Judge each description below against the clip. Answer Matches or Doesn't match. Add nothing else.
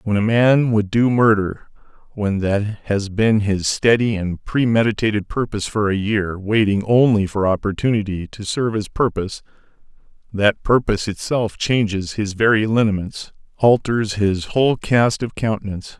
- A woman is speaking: Doesn't match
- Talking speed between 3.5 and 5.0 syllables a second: Matches